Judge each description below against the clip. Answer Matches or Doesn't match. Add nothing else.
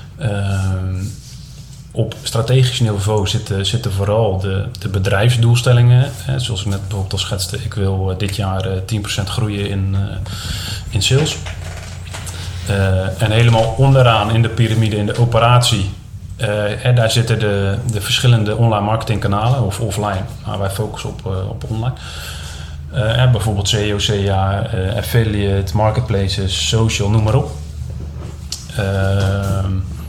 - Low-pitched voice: Matches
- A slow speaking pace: Matches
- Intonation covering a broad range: Doesn't match